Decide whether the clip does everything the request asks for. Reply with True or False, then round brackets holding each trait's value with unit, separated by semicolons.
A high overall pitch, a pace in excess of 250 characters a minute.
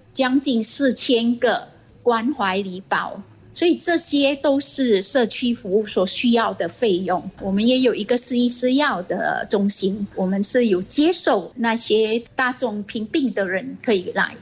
False (235 Hz; 230 characters per minute)